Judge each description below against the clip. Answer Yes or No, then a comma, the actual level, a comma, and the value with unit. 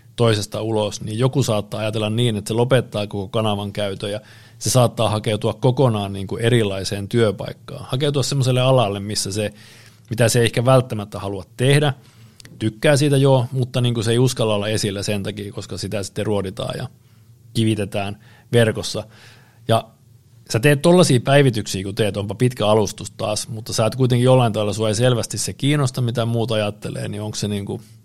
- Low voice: Yes, low, 115 Hz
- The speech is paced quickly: Yes, fast, 180 wpm